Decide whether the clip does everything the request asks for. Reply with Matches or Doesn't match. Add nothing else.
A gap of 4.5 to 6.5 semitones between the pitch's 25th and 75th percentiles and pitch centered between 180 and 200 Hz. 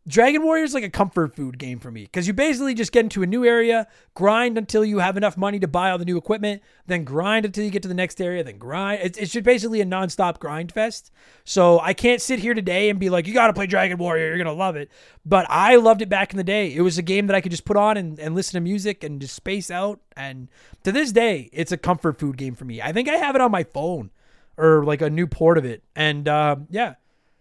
Matches